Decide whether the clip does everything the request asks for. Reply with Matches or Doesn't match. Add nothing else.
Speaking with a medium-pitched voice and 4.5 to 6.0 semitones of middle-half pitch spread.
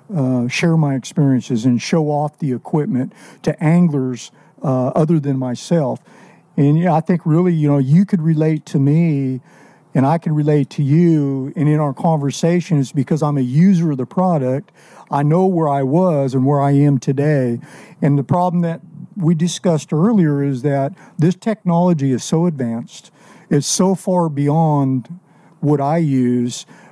Doesn't match